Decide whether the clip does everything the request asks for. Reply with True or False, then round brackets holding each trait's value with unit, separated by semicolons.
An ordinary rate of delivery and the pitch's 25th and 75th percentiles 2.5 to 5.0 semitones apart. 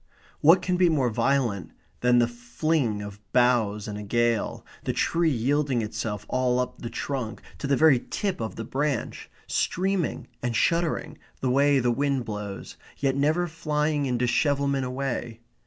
True (160 wpm; 4.1 semitones)